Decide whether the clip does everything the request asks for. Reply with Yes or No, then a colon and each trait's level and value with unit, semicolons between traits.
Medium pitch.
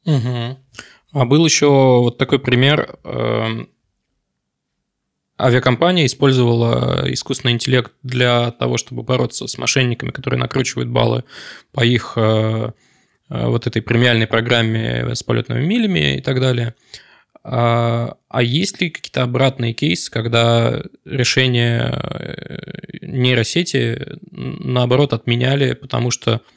No: low, 125 Hz